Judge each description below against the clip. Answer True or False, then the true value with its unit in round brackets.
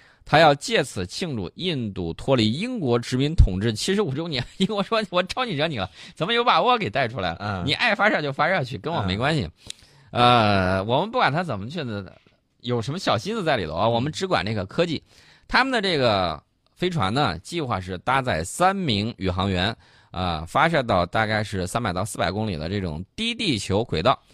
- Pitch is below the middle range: True (115 Hz)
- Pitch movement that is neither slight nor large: False (8.6 semitones)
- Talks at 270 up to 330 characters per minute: True (305 characters per minute)